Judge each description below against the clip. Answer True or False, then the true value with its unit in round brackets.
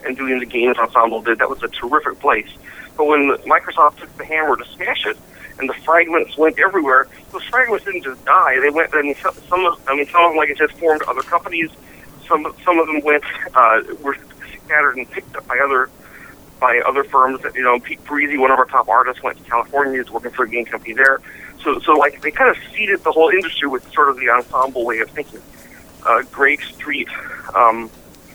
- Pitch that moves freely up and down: False (4.2 semitones)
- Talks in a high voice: False (140 Hz)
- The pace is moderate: False (225 wpm)